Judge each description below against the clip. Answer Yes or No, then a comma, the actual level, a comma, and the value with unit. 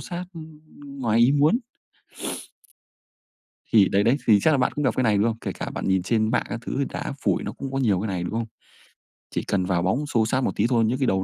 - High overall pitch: No, low, 115 Hz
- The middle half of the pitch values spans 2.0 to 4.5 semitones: No, average, 5.0 semitones